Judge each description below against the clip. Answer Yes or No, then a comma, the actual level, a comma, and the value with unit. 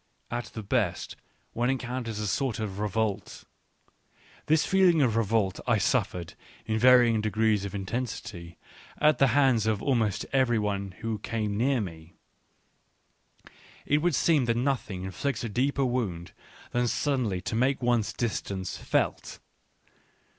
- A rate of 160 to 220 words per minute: No, average, 140 wpm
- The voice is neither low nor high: No, low, 115 Hz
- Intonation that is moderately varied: Yes, average, 4.0 semitones